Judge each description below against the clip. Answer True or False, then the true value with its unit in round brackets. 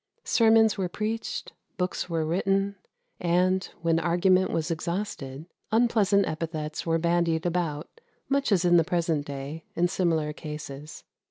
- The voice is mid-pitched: True (175 Hz)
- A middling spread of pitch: True (3.2 semitones)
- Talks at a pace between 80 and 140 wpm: True (135 wpm)